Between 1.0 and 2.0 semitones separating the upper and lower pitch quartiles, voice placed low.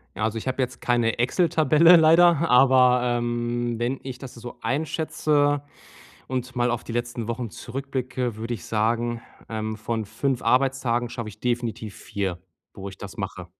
No: narrow, 2.4 semitones; low, 120 Hz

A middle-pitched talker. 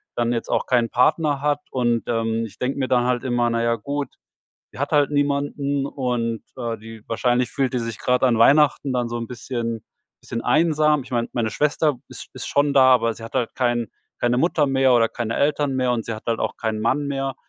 No: low, 125 Hz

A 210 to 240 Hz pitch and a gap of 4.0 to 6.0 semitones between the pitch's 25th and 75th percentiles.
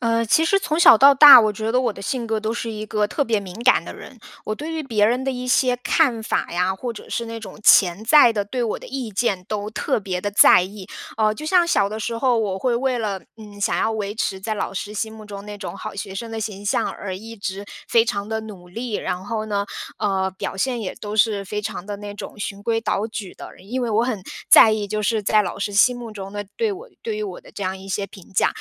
No: high, 215 Hz; average, 2.9 semitones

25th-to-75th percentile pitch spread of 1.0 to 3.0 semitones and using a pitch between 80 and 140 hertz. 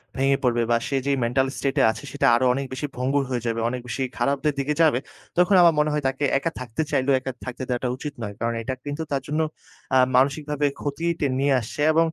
Yes: average, 2.7 semitones; low, 135 Hz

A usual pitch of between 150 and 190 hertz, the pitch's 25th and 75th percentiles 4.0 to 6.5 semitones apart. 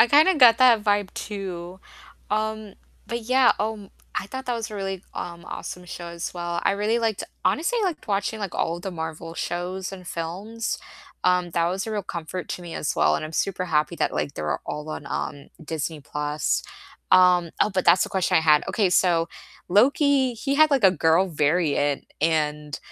Yes: medium, 185 Hz; average, 4.6 semitones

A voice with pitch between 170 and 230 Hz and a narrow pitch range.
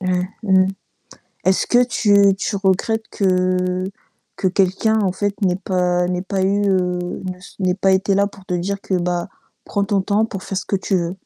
Yes: high, 190 Hz; narrow, 1.7 semitones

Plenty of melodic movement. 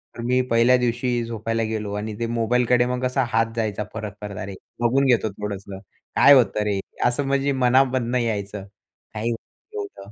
No: average, 2.9 semitones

